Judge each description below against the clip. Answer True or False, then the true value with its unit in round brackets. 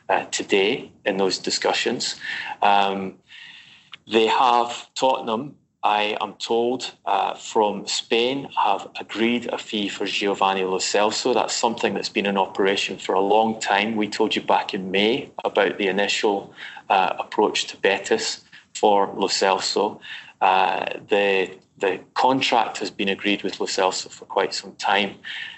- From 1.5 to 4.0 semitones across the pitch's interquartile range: True (3.3 semitones)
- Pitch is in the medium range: False (110 Hz)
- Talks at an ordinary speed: True (145 wpm)